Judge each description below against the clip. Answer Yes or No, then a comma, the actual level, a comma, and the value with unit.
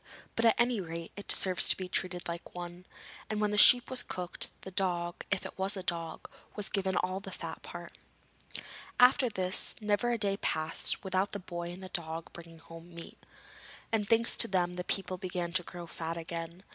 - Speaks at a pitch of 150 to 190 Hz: Yes, medium, 185 Hz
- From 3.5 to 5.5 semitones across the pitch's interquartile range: No, average, 2.9 semitones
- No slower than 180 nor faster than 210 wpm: Yes, average, 200 wpm